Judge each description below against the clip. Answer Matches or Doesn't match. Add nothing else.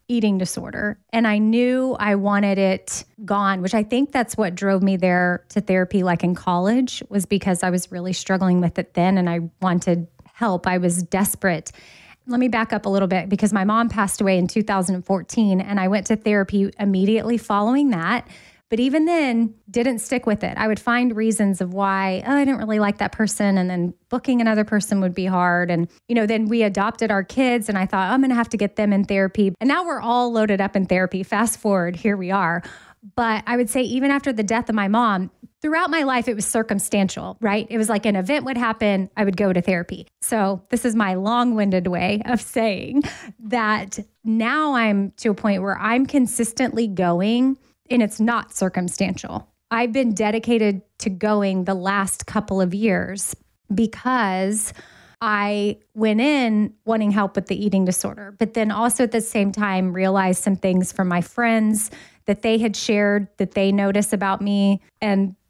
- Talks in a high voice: Matches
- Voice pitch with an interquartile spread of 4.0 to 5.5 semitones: Doesn't match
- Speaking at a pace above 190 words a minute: Matches